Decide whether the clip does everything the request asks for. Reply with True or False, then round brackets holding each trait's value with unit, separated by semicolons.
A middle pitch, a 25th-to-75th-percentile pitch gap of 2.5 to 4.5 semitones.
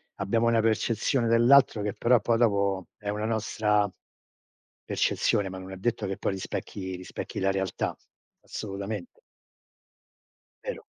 False (105 Hz; 2.9 semitones)